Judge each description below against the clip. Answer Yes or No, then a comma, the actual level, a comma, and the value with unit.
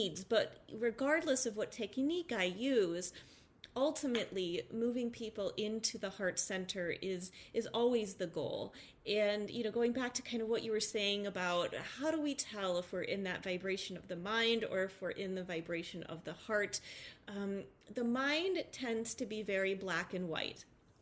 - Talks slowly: No, average, 185 wpm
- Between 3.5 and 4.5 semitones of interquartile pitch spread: Yes, average, 4.2 semitones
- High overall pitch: Yes, high, 210 Hz